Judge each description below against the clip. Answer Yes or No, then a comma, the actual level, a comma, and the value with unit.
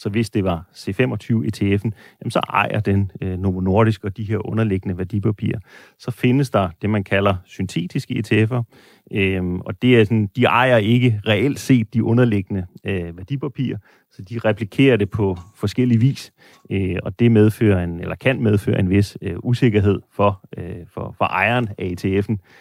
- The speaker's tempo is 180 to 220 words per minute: No, average, 170 wpm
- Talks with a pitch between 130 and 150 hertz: No, low, 105 Hz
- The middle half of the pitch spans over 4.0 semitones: No, average, 3.3 semitones